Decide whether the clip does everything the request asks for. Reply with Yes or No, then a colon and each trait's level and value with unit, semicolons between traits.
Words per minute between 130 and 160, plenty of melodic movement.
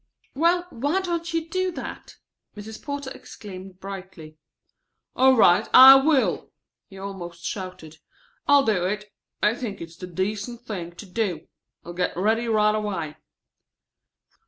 Yes: slow, 135 wpm; wide, 6.3 semitones